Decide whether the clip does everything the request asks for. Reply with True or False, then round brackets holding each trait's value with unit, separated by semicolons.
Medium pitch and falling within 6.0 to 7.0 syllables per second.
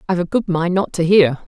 True (180 Hz; 6.1 syllables/s)